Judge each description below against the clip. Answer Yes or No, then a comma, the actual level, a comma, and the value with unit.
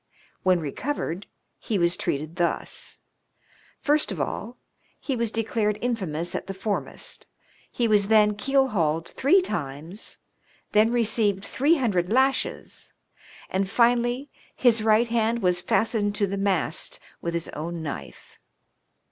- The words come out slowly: Yes, slow, 130 wpm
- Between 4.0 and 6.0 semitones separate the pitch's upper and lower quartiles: Yes, average, 5.1 semitones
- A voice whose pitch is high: Yes, high, 210 Hz